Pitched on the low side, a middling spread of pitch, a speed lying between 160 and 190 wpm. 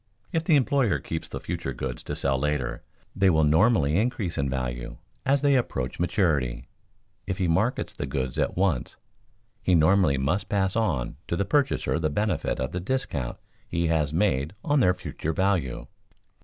No: very low, 85 Hz; wide, 6.8 semitones; average, 170 wpm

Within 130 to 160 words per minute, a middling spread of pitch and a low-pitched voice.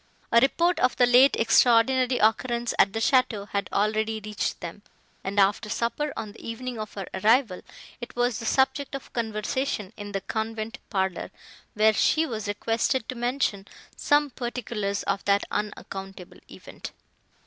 No: average, 155 wpm; average, 3.4 semitones; high, 225 Hz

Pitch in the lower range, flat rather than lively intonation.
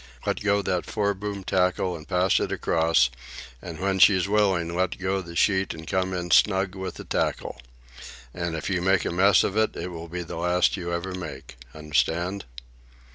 Yes: very low, 90 Hz; narrow, 2.2 semitones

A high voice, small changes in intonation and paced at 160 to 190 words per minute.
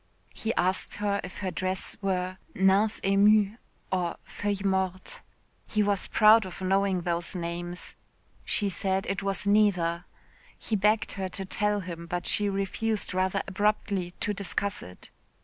No: high, 195 Hz; narrow, 2.0 semitones; average, 150 wpm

